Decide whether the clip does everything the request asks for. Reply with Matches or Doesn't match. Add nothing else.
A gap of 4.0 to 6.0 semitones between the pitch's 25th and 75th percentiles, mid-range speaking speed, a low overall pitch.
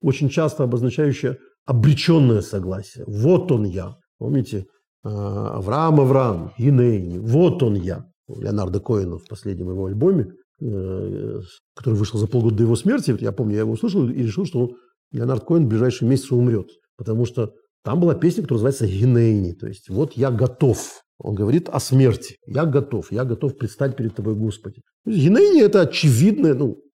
Doesn't match